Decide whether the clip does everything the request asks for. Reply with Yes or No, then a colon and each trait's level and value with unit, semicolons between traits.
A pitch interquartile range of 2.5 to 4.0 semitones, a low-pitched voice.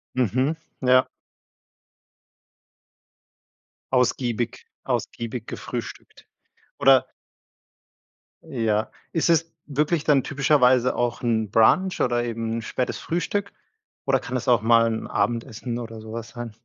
Yes: average, 2.9 semitones; low, 120 Hz